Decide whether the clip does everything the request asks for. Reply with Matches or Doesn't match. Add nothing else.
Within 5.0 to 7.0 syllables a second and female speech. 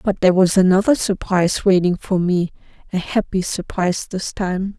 Matches